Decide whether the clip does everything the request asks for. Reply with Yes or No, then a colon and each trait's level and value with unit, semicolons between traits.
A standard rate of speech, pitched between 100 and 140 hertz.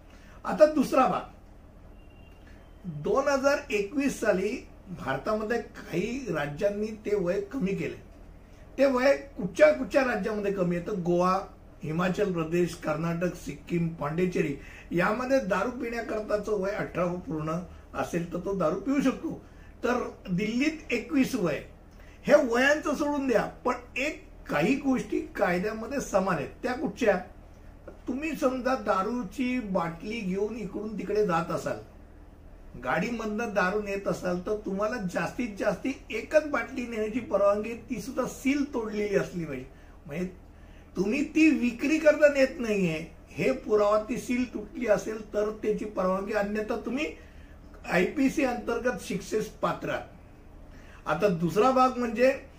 No: average, 125 wpm; high, 210 Hz